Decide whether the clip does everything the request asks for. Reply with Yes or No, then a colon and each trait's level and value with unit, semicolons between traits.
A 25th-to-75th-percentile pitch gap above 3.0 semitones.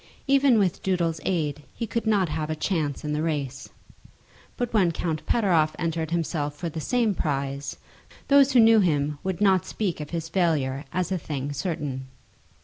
Yes: average, 4.5 semitones